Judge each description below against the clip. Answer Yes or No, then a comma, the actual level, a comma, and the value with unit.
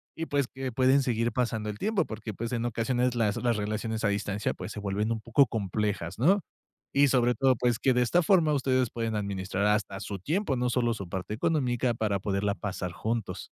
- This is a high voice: No, low, 115 Hz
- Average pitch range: Yes, average, 3.7 semitones